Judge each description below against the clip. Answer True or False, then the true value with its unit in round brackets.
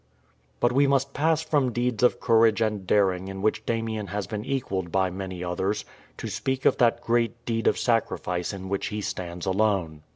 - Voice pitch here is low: True (105 Hz)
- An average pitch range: True (4.1 semitones)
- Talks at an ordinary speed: True (190 wpm)